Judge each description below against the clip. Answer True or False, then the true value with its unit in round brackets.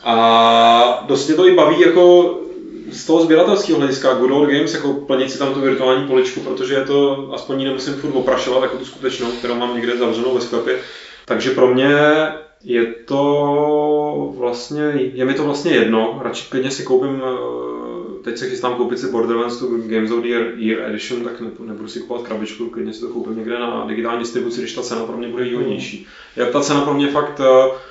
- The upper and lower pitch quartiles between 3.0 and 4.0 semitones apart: True (3.3 semitones)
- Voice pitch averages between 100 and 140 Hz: True (130 Hz)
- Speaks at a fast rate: True (195 wpm)